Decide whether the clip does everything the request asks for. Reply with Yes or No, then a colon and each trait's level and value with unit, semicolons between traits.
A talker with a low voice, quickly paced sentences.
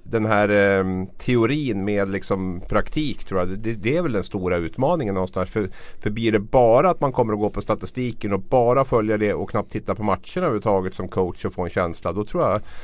Yes: low, 105 Hz; fast, 225 wpm